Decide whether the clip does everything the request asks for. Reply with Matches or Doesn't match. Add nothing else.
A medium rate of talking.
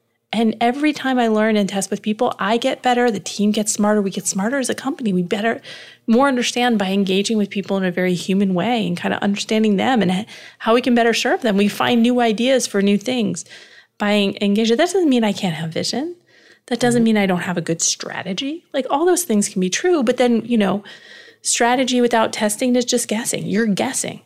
Doesn't match